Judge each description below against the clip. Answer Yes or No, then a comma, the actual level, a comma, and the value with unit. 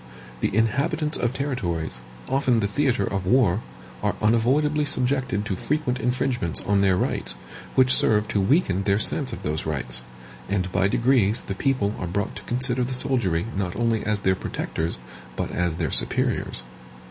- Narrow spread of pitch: No, average, 5.3 semitones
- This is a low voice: Yes, low, 110 Hz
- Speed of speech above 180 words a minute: No, average, 165 wpm